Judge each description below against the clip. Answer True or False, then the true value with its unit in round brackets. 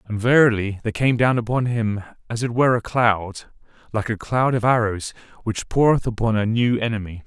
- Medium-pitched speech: False (115 Hz)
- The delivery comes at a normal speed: True (190 wpm)